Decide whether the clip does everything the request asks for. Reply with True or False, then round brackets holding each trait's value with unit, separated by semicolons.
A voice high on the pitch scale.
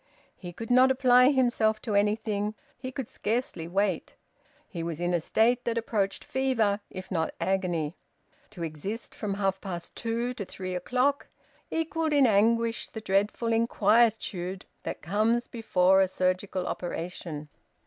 True (210 Hz)